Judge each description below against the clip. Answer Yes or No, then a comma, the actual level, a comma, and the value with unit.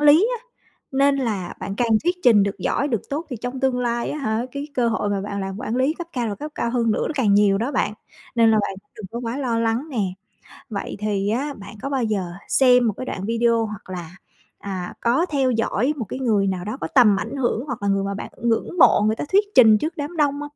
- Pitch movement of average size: Yes, average, 4.6 semitones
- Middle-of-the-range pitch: No, high, 230 Hz